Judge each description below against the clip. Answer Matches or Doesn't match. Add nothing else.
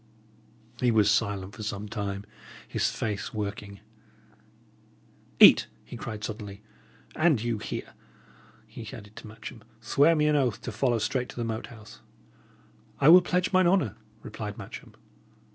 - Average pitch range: Matches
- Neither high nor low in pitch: Doesn't match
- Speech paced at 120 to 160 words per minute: Matches